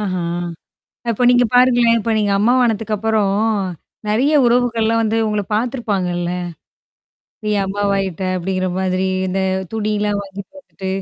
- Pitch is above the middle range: Yes, high, 210 Hz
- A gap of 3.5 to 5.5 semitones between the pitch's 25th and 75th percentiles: No, average, 3.1 semitones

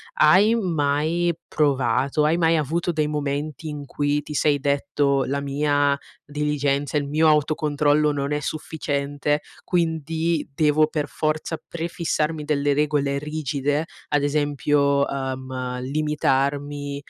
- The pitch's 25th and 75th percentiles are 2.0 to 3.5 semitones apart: No, narrow, 1.5 semitones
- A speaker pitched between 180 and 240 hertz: No, medium, 145 Hz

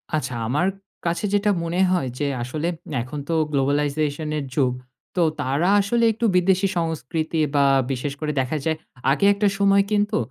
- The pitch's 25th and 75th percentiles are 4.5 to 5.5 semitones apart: Yes, average, 5.1 semitones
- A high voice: No, medium, 160 Hz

